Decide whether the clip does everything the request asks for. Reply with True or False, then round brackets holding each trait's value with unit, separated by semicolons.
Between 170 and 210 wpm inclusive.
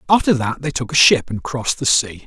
False (265 wpm)